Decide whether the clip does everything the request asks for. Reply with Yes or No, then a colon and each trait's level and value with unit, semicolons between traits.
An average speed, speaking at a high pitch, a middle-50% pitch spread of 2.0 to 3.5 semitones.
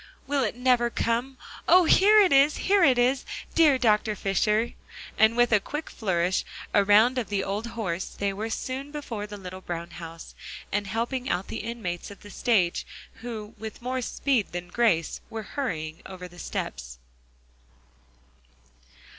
No: average, 160 wpm; high, 220 Hz; average, 4.8 semitones